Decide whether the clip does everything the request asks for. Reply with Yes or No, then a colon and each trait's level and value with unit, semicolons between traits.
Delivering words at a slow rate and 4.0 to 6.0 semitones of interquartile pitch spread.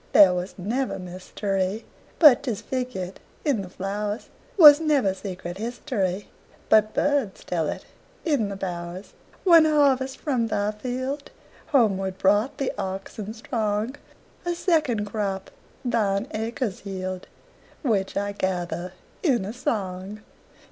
Yes: slow, 105 wpm; average, 5.1 semitones